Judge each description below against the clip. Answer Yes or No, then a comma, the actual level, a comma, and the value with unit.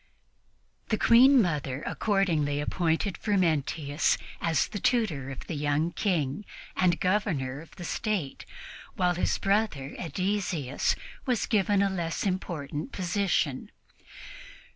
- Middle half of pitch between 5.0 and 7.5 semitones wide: Yes, wide, 5.4 semitones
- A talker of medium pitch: Yes, medium, 175 Hz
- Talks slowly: Yes, slow, 115 wpm